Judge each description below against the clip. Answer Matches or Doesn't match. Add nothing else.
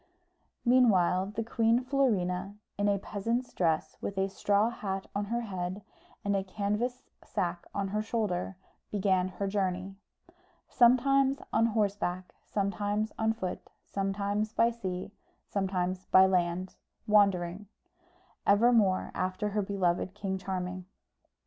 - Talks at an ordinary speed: Doesn't match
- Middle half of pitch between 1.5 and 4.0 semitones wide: Matches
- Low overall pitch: Doesn't match